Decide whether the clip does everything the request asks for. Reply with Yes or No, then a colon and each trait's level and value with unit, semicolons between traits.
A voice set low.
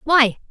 No: very high, 265 Hz